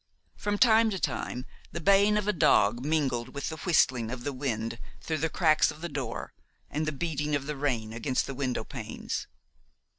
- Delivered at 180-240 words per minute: Yes, average, 190 wpm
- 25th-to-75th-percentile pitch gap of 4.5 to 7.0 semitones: Yes, average, 4.8 semitones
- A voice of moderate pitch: Yes, medium, 145 Hz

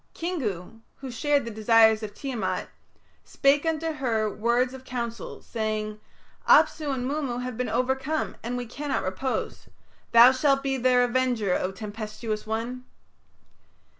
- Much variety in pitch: No, average, 3.5 semitones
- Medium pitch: No, high, 245 Hz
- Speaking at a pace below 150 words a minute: Yes, slow, 135 wpm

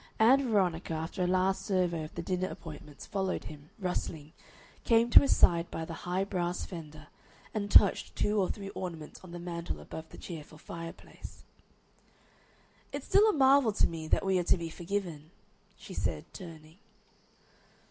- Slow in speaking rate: No, average, 170 wpm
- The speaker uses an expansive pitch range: No, average, 3.4 semitones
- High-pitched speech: No, medium, 180 Hz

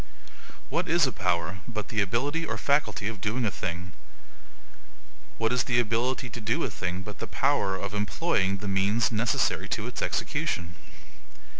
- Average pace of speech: Yes, average, 165 wpm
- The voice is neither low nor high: No, low, 110 Hz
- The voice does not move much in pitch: No, average, 3.9 semitones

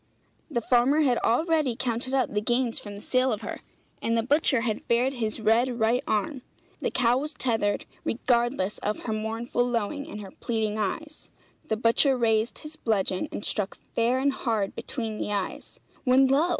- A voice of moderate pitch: No, high, 235 Hz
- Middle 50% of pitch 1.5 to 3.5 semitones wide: Yes, average, 3.2 semitones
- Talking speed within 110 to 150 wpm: No, average, 180 wpm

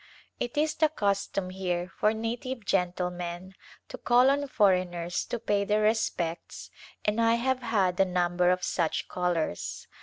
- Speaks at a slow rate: No, average, 150 wpm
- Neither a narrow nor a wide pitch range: Yes, average, 4.5 semitones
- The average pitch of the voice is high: Yes, high, 195 Hz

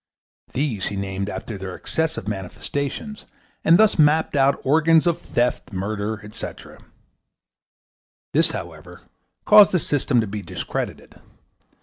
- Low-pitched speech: Yes, low, 130 Hz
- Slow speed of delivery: Yes, slow, 120 wpm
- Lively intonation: Yes, wide, 7.8 semitones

